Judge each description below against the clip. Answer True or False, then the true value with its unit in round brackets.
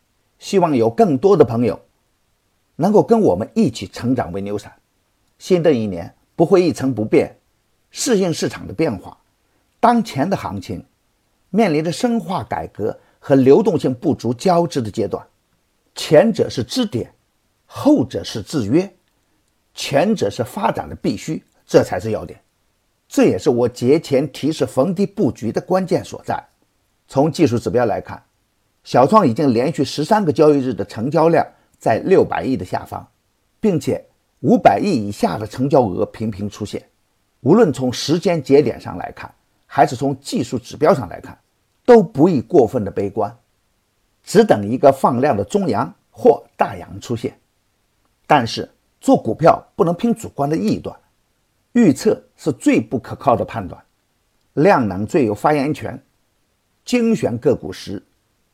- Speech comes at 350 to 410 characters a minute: False (230 characters per minute)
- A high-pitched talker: False (135 Hz)